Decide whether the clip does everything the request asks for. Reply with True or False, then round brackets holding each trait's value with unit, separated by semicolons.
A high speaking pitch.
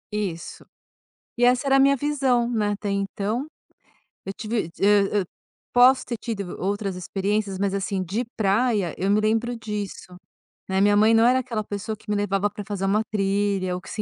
True (205 Hz)